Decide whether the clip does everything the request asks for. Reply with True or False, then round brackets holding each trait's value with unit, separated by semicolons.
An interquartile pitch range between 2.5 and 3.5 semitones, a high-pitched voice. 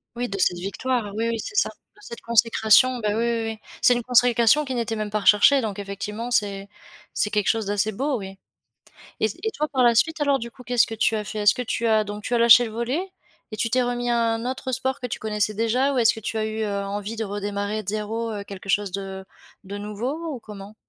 True (2.9 semitones; 225 Hz)